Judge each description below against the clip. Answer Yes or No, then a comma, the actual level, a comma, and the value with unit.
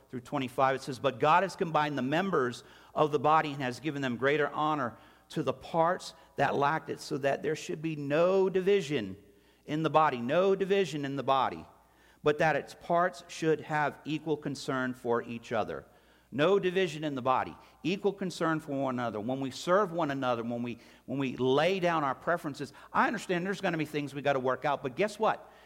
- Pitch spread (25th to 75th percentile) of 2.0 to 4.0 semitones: No, average, 4.7 semitones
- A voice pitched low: No, medium, 150 Hz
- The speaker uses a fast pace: Yes, fast, 210 wpm